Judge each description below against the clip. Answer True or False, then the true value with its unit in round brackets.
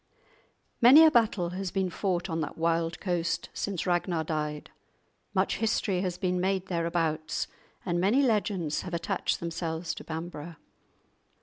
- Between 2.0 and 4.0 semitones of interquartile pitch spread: True (2.7 semitones)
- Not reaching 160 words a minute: True (140 wpm)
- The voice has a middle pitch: True (175 Hz)